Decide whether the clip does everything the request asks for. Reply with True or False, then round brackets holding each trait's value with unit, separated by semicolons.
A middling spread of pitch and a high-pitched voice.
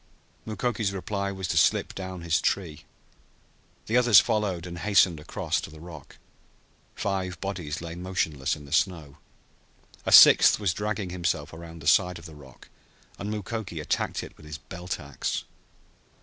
False (3.8 semitones; 90 Hz)